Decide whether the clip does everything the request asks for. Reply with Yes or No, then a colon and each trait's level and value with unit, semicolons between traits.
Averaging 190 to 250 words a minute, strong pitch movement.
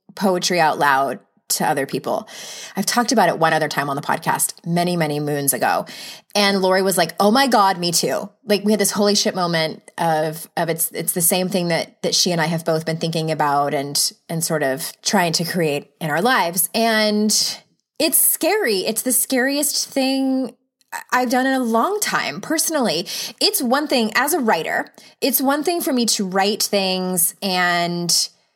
Yes: average, 195 wpm; wide, 6.7 semitones